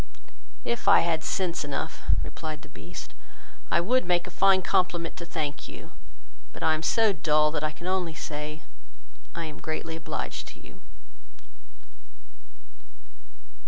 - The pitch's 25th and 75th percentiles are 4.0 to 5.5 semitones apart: No, average, 2.7 semitones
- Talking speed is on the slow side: No, average, 145 wpm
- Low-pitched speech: No, medium, 165 Hz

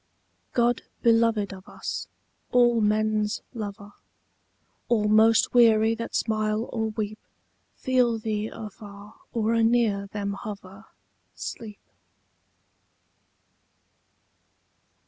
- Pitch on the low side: No, high, 215 Hz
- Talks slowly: Yes, slow, 90 wpm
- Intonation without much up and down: Yes, narrow, 1.6 semitones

